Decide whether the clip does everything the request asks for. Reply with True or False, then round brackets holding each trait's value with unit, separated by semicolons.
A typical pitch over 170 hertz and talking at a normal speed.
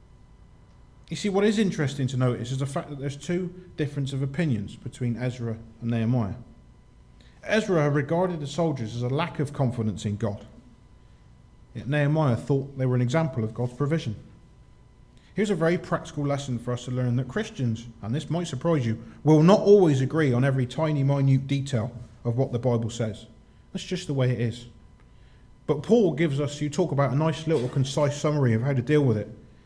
False (135 Hz; 190 wpm)